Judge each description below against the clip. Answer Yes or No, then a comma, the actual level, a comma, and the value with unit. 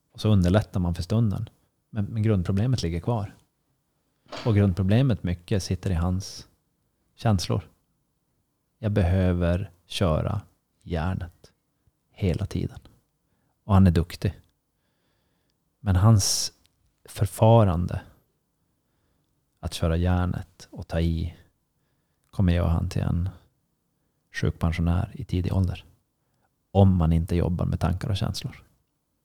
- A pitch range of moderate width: Yes, average, 4.3 semitones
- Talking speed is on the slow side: Yes, slow, 110 wpm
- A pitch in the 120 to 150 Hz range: No, very low, 95 Hz